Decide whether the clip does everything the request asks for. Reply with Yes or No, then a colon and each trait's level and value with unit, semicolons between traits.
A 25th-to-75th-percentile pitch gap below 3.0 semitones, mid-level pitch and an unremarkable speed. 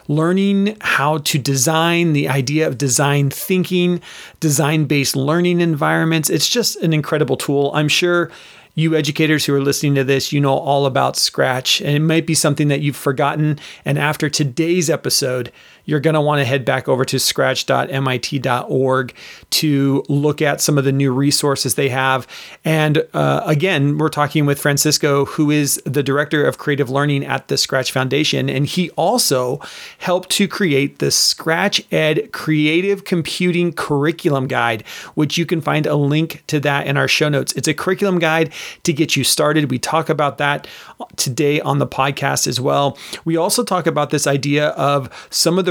Yes: narrow, 2.6 semitones; medium, 150 Hz; average, 175 wpm